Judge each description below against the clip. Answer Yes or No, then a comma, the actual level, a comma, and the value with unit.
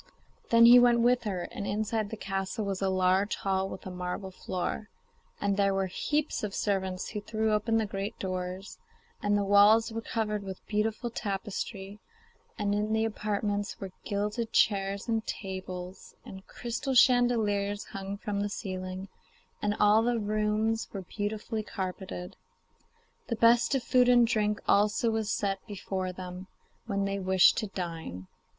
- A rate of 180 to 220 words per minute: No, average, 160 wpm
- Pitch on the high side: Yes, high, 205 Hz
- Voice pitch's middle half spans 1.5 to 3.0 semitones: Yes, narrow, 2.4 semitones